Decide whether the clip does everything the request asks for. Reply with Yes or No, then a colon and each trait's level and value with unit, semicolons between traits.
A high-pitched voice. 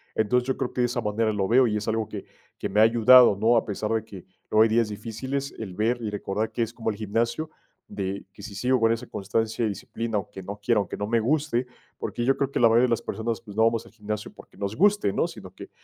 No: low, 110 Hz